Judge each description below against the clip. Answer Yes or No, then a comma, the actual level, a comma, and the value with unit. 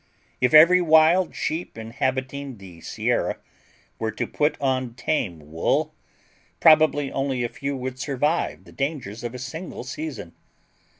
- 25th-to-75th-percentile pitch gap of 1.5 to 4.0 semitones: No, average, 4.5 semitones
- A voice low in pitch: Yes, low, 130 Hz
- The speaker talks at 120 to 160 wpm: Yes, slow, 135 wpm